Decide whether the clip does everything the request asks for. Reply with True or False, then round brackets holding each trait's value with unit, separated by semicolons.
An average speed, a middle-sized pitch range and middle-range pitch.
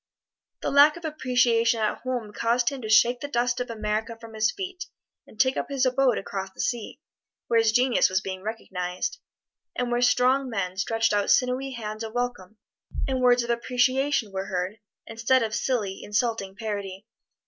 False (180 wpm; 3.2 semitones; 235 Hz)